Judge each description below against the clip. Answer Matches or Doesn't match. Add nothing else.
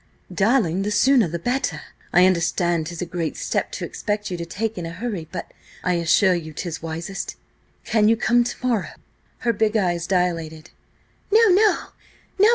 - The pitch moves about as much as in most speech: Matches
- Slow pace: Doesn't match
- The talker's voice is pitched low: Doesn't match